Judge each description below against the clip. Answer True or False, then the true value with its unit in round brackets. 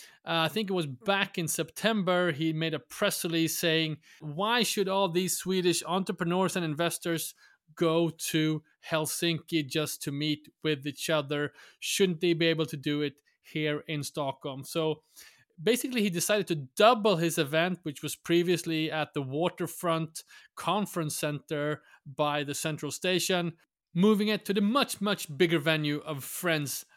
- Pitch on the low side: False (165 Hz)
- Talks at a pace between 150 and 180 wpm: True (160 wpm)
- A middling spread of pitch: True (3.0 semitones)